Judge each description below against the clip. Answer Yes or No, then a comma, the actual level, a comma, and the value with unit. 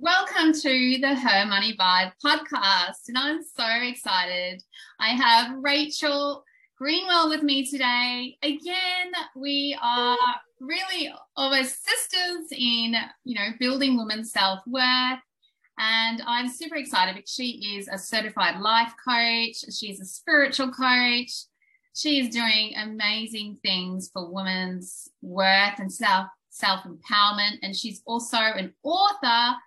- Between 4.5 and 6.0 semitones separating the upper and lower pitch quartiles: Yes, wide, 5.5 semitones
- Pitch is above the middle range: Yes, high, 245 Hz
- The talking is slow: Yes, slow, 120 wpm